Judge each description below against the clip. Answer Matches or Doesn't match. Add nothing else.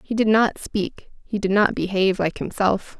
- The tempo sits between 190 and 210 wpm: Matches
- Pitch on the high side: Matches